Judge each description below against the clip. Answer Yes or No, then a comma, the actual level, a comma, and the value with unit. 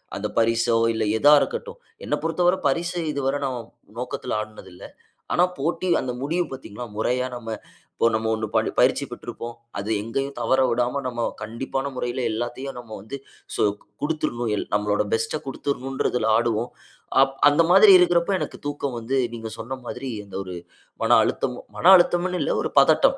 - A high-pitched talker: No, low, 125 Hz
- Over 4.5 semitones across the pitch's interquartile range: No, average, 4.1 semitones